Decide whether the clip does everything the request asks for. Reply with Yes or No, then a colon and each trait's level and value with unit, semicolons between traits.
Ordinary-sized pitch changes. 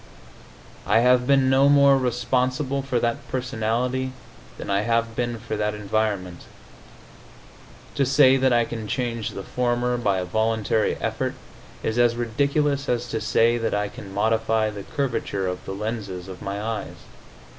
Yes: average, 3.2 semitones